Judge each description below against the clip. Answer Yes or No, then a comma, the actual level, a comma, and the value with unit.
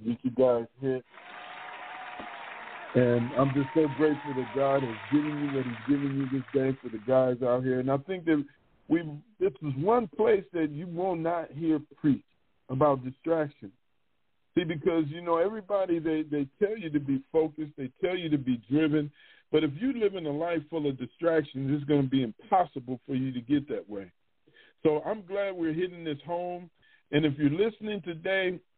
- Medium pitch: Yes, medium, 150 Hz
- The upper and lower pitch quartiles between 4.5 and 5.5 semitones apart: No, average, 4.1 semitones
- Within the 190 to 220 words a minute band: Yes, average, 195 wpm